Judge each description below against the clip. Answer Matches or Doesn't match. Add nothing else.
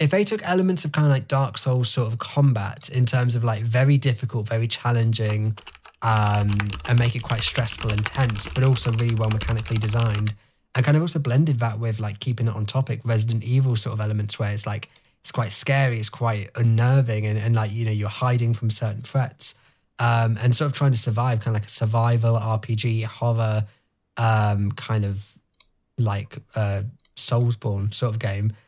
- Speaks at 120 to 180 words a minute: Doesn't match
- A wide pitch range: Doesn't match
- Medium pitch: Doesn't match